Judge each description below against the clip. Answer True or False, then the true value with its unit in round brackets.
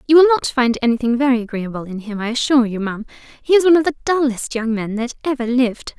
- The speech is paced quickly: True (240 wpm)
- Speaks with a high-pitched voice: True (250 Hz)